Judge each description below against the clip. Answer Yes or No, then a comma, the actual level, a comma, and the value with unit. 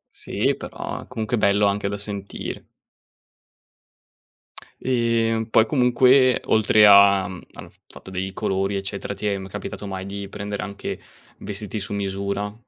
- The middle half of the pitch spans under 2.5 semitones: Yes, narrow, 1.9 semitones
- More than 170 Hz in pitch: No, low, 100 Hz